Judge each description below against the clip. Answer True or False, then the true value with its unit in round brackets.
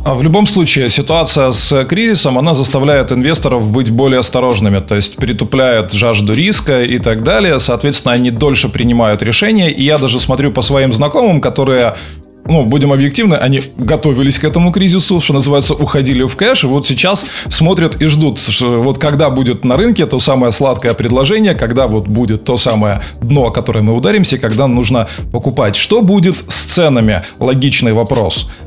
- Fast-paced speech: True (170 wpm)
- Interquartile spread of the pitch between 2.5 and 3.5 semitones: False (4.0 semitones)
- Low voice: True (130 Hz)